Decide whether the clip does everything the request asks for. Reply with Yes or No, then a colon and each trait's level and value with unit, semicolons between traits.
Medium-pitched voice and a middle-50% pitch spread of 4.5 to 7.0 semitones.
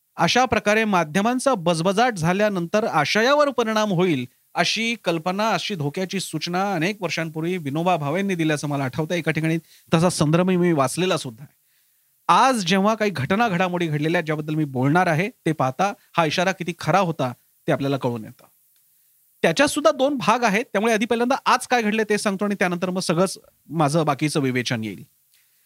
Yes: medium, 180 Hz; average, 5.1 semitones